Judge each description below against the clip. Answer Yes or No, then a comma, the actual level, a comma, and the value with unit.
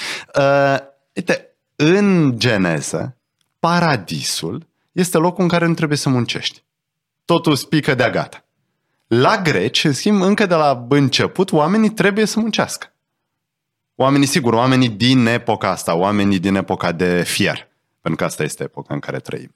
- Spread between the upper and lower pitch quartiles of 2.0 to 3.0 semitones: No, average, 5.2 semitones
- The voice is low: No, medium, 145 Hz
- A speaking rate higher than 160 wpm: No, average, 145 wpm